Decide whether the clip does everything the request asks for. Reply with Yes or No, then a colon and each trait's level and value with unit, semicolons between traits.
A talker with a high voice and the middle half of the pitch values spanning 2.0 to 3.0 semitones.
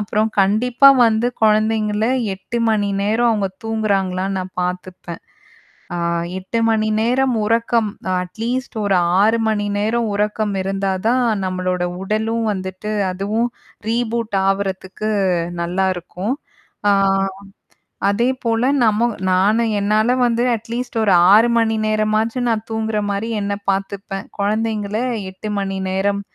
Yes: high, 215 Hz; narrow, 2.6 semitones